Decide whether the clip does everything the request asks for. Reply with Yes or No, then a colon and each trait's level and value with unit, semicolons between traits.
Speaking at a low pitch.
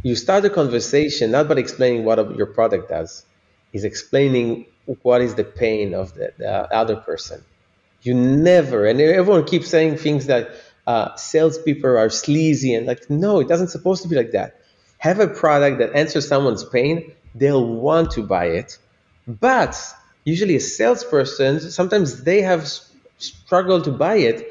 No: medium, 145 Hz